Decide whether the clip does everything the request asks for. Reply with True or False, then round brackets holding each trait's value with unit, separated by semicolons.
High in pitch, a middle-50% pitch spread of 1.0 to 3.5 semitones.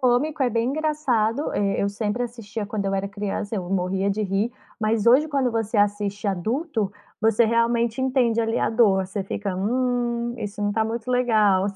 True (225 Hz; 3.2 semitones)